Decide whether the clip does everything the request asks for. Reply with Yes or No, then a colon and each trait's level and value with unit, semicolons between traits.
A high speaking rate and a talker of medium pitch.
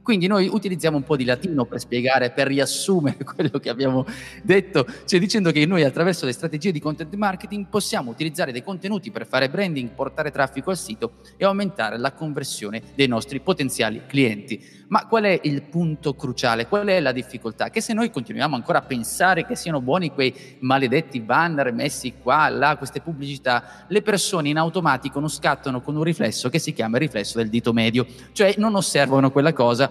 Yes: fast, 190 wpm; medium, 145 Hz